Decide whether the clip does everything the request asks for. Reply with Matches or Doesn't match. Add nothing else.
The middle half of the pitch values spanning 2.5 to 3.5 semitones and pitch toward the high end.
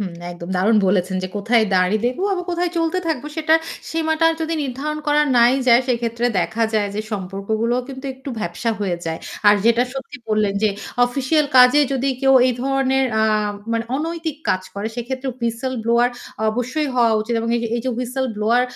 Doesn't match